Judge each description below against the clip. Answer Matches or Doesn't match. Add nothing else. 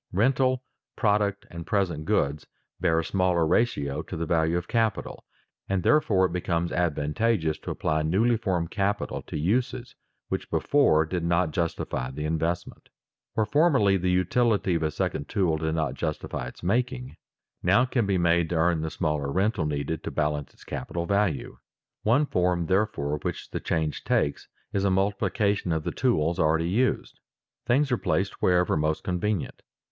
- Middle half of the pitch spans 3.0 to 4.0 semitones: Doesn't match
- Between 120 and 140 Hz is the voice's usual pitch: Doesn't match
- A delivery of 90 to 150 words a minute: Doesn't match